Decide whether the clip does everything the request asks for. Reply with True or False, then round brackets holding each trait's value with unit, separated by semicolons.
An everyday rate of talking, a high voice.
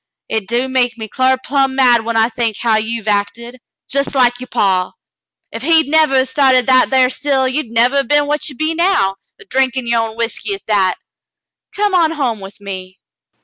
False (210 wpm; 255 Hz)